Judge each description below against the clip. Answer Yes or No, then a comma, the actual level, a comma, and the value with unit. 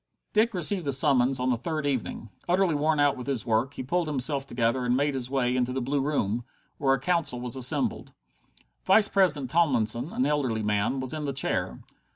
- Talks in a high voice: No, low, 135 Hz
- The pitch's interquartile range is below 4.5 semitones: Yes, average, 3.5 semitones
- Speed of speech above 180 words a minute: Yes, average, 200 wpm